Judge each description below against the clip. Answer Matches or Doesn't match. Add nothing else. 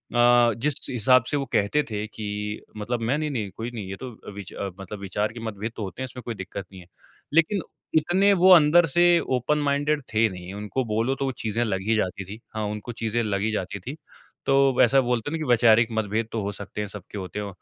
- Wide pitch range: Doesn't match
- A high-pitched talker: Doesn't match